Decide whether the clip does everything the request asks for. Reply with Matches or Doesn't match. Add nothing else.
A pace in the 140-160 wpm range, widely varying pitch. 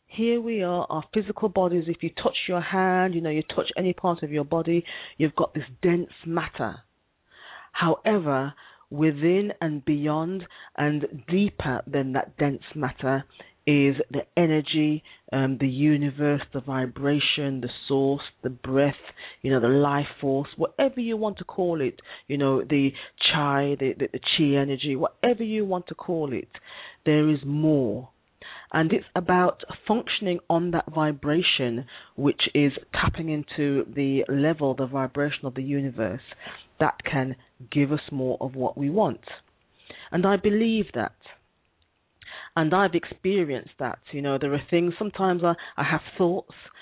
Doesn't match